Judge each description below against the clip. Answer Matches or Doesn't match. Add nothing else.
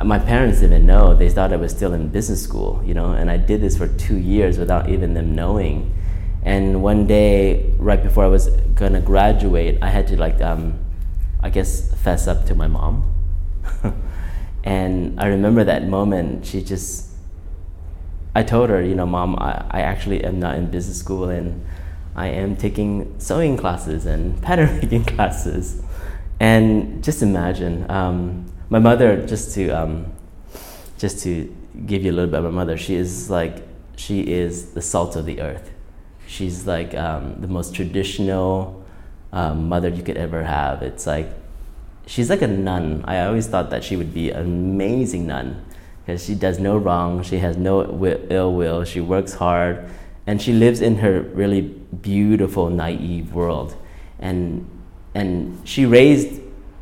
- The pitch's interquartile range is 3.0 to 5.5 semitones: Doesn't match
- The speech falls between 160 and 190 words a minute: Matches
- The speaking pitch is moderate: Doesn't match